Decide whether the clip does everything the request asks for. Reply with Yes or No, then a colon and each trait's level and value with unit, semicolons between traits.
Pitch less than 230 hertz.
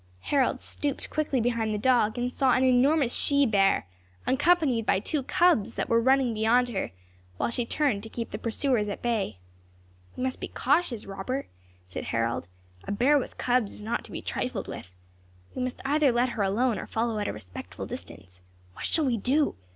No: high, 245 Hz